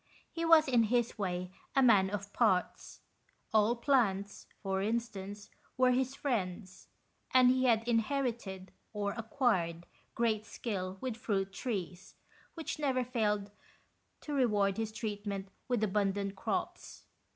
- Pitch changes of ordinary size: Yes, average, 4.0 semitones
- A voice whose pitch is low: No, high, 215 Hz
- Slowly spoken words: Yes, slow, 130 wpm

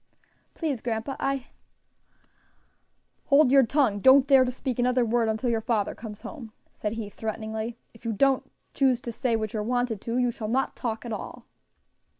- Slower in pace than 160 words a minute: No, average, 180 wpm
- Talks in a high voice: Yes, high, 235 Hz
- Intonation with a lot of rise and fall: No, average, 3.0 semitones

